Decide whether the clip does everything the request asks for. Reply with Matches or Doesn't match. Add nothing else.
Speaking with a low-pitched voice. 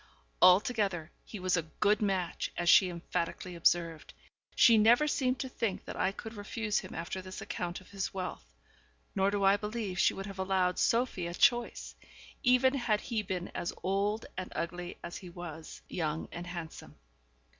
Doesn't match